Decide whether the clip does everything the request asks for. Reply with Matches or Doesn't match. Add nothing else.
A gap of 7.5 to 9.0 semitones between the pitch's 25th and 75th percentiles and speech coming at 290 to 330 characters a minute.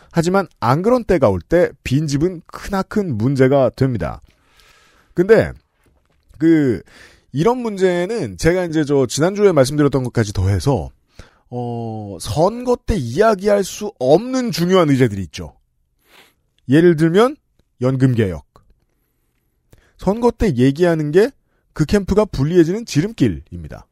Doesn't match